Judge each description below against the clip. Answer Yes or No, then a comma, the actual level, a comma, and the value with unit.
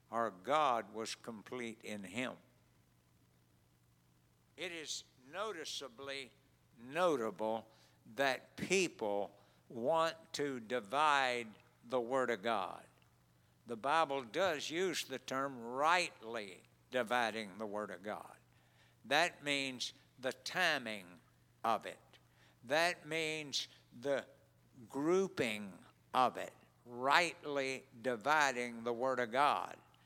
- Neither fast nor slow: No, slow, 100 wpm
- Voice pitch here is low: Yes, low, 125 Hz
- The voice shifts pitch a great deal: No, average, 4.7 semitones